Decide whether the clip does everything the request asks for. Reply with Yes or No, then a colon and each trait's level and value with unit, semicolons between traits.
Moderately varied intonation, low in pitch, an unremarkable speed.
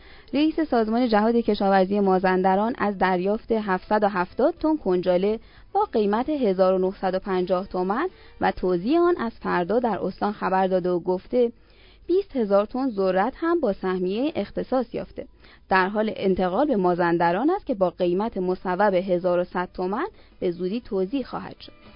No: average, 4.8 semitones; high, 200 Hz; average, 140 wpm